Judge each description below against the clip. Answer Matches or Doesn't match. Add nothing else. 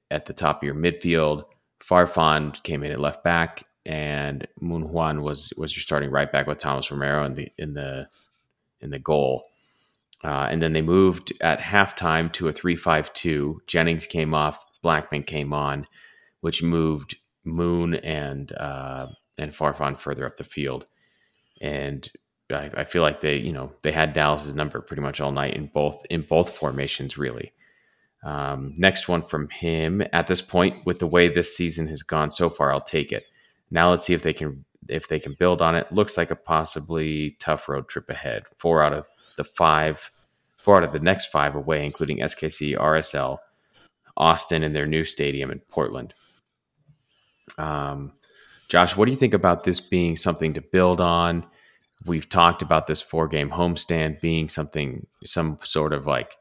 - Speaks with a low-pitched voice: Matches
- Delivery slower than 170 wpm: Doesn't match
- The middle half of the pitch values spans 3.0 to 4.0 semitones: Doesn't match